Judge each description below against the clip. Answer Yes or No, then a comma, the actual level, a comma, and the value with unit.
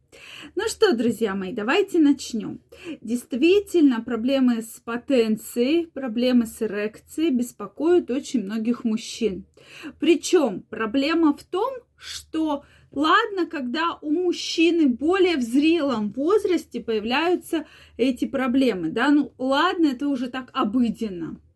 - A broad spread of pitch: Yes, wide, 5.7 semitones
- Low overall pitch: No, very high, 275 Hz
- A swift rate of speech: No, slow, 110 wpm